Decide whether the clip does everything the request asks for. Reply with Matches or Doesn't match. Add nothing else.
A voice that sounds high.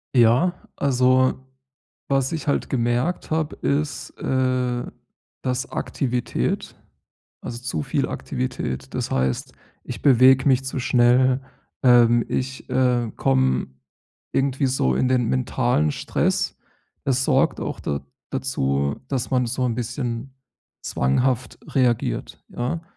Doesn't match